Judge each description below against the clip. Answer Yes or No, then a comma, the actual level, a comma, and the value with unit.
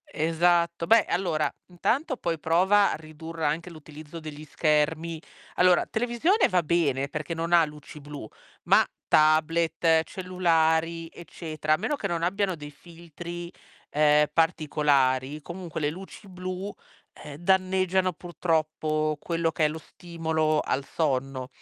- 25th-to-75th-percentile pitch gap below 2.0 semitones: No, narrow, 2.5 semitones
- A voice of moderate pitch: Yes, medium, 165 Hz